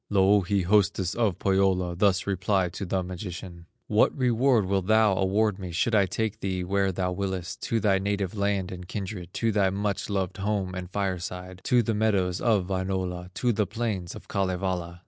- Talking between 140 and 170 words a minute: No, average, 180 wpm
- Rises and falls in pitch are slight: Yes, narrow, 2.1 semitones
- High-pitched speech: No, very low, 95 Hz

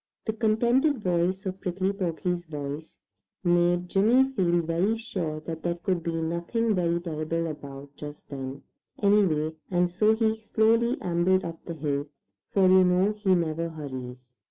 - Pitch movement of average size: Yes, average, 4.1 semitones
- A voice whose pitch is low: No, medium, 175 Hz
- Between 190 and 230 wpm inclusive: No, average, 155 wpm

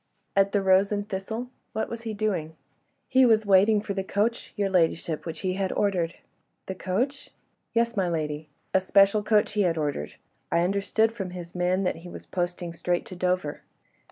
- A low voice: No, high, 190 Hz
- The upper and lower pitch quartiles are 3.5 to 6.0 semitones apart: No, average, 2.9 semitones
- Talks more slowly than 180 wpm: No, average, 185 wpm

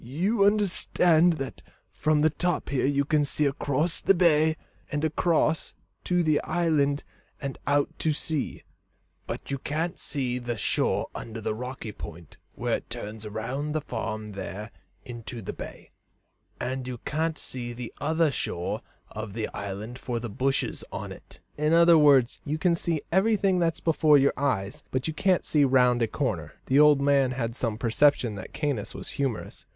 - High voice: No, medium, 140 Hz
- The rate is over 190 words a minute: No, average, 170 wpm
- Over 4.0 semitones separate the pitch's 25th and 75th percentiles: Yes, average, 4.8 semitones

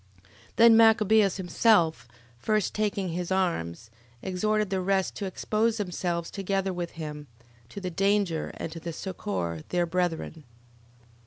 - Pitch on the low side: No, medium, 185 Hz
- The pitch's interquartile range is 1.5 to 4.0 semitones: Yes, average, 3.7 semitones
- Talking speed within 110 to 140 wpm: Yes, slow, 135 wpm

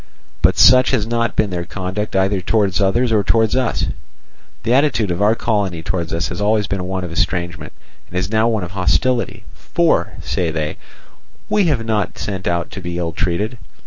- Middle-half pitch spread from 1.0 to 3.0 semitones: No, average, 4.1 semitones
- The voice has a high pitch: No, low, 100 Hz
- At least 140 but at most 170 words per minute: No, average, 190 wpm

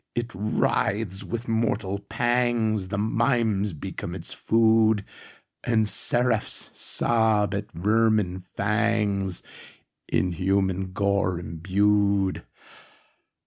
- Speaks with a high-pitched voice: No, low, 105 Hz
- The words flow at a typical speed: No, slow, 70 wpm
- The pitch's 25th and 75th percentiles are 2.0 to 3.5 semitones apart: Yes, narrow, 2.6 semitones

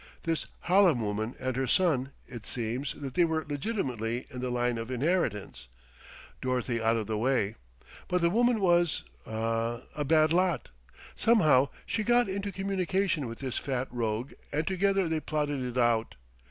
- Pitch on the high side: No, low, 135 Hz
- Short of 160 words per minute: No, average, 165 wpm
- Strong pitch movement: Yes, wide, 6.8 semitones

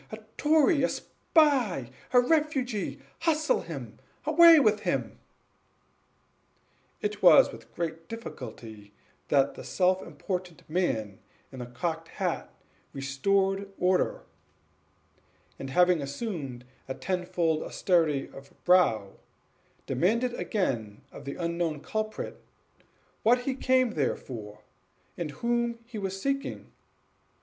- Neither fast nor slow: No, slow, 110 wpm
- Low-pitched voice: No, medium, 180 Hz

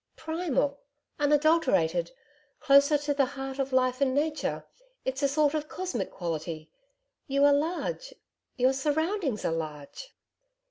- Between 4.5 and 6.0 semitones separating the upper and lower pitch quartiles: No, average, 3.2 semitones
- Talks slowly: Yes, slow, 130 wpm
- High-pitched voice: Yes, very high, 280 Hz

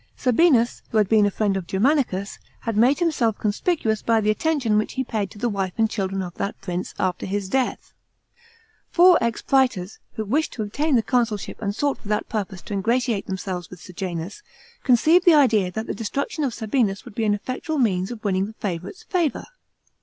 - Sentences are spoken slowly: No, average, 200 wpm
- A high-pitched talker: Yes, high, 220 Hz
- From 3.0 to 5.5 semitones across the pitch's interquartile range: Yes, average, 4.7 semitones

